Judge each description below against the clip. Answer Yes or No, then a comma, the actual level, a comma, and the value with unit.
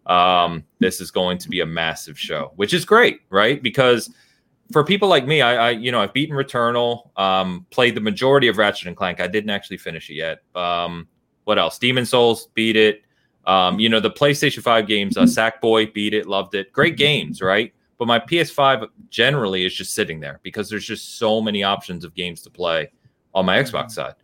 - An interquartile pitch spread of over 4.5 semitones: Yes, average, 4.9 semitones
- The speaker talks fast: Yes, fast, 210 wpm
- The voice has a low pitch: Yes, low, 110 Hz